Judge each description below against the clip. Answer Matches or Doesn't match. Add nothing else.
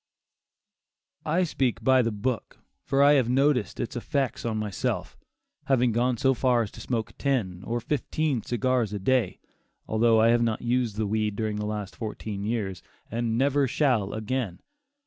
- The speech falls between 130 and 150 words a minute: Doesn't match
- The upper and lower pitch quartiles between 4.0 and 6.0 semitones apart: Doesn't match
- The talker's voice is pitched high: Doesn't match